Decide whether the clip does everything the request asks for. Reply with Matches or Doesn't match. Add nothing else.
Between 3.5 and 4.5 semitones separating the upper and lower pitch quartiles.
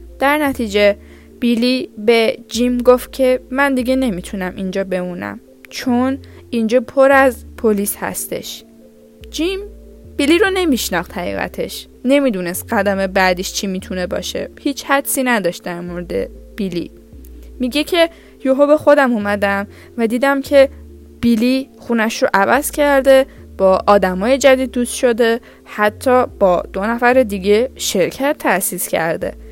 Doesn't match